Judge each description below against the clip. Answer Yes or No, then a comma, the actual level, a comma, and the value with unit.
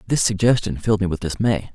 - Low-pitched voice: Yes, low, 100 Hz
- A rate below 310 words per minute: Yes, fast, 205 wpm